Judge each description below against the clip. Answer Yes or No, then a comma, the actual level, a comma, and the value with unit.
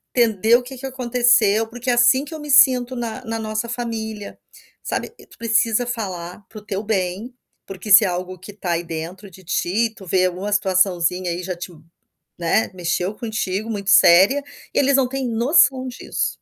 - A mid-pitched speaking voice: No, high, 215 Hz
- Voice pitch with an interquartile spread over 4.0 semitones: Yes, average, 4.6 semitones